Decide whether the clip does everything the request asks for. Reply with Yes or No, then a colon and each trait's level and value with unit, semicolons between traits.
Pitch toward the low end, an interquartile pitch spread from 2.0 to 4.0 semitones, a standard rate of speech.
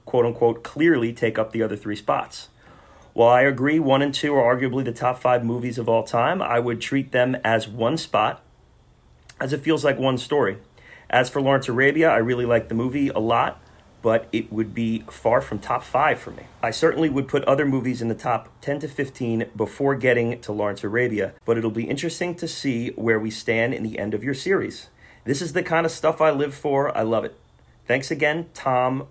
No: low, 125 Hz; average, 3.7 semitones; fast, 215 wpm